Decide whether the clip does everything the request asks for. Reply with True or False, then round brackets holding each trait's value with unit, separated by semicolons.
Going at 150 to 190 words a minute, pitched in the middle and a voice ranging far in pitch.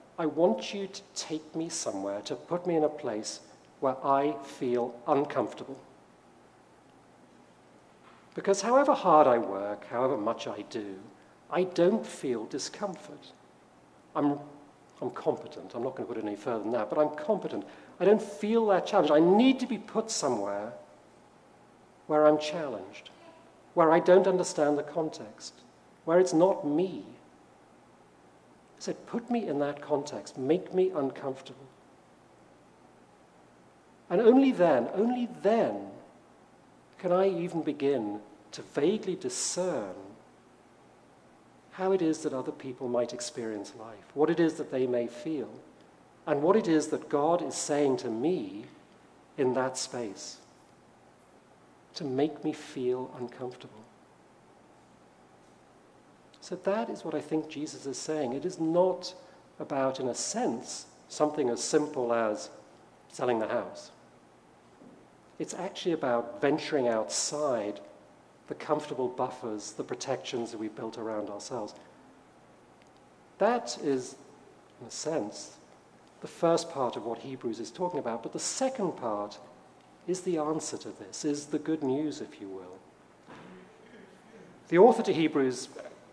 False (140 wpm; 150 Hz; 6.4 semitones)